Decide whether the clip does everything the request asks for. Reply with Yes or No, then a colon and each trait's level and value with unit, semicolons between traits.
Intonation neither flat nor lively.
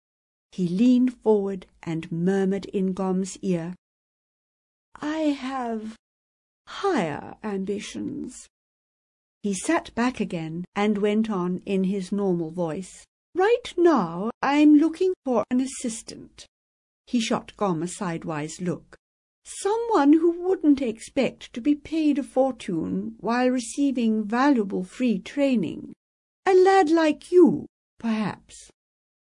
No: wide, 6.9 semitones